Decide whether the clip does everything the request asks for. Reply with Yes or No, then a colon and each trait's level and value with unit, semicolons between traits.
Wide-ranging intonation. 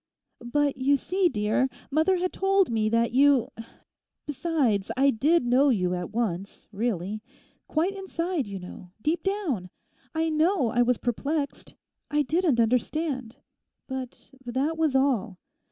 Yes: wide, 5.9 semitones